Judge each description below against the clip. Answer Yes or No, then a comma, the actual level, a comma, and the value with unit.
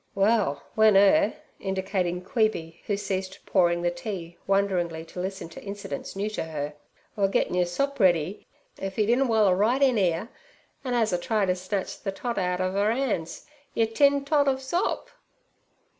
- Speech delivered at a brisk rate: No, average, 170 wpm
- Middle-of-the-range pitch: No, high, 195 Hz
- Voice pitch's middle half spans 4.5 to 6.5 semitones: No, average, 3.8 semitones